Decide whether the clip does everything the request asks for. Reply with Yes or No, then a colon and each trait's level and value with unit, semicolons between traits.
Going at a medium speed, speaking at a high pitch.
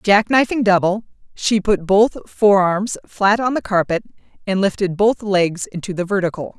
Yes: average, 155 wpm; high, 200 Hz